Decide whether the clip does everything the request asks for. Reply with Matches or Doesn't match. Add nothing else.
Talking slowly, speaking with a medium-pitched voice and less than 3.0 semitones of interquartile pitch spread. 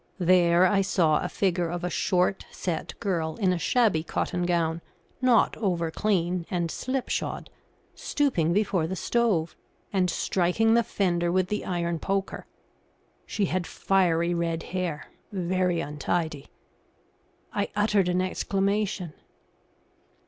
Matches